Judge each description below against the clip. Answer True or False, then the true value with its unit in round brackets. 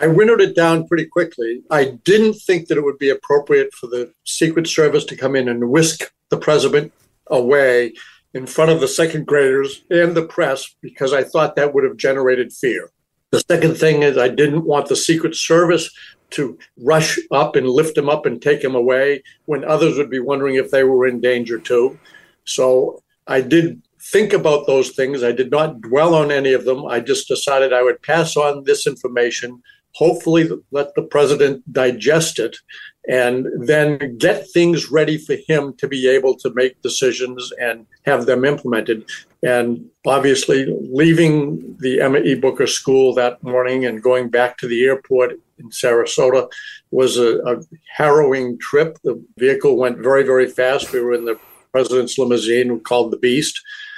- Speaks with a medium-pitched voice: True (145 Hz)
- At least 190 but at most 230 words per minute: False (180 wpm)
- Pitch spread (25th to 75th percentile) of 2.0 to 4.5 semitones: False (5.1 semitones)